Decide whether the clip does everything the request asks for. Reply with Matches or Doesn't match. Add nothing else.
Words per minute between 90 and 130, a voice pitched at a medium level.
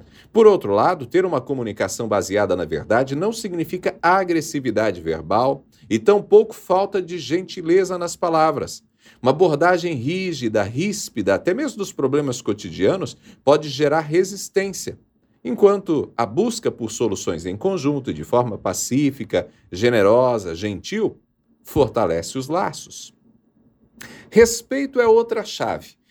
Matches